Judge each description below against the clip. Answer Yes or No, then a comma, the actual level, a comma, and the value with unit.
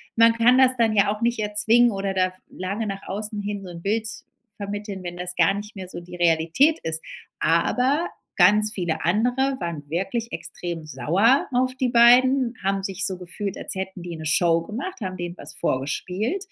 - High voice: Yes, high, 200 Hz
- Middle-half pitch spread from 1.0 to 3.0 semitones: No, average, 4.8 semitones